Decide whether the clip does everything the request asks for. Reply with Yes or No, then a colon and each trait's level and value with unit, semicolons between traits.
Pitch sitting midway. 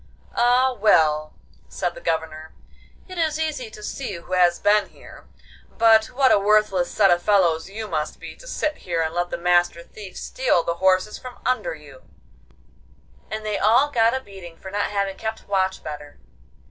No: high, 200 Hz